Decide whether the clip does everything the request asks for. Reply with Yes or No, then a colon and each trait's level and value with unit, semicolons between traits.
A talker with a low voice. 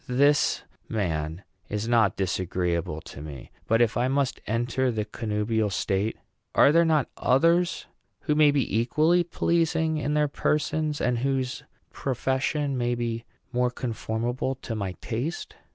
Yes: low, 125 Hz